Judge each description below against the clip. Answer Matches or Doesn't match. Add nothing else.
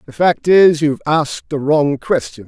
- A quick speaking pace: Doesn't match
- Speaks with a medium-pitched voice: Matches